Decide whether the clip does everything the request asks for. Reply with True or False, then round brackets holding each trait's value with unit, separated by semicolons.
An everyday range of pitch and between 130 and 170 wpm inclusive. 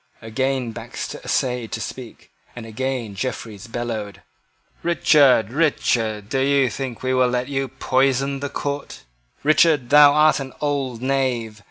True (3.1 semitones; 140 wpm)